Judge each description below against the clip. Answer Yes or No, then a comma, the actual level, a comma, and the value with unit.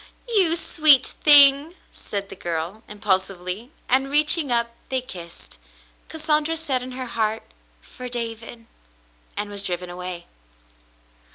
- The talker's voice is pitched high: Yes, high, 235 Hz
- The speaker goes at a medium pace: No, slow, 120 wpm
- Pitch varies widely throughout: Yes, wide, 6.6 semitones